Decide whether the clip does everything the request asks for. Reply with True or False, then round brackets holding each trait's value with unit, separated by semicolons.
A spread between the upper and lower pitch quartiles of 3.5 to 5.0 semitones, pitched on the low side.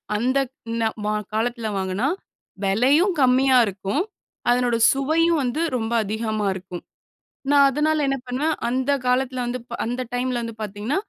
False (3.8 semitones; 250 Hz)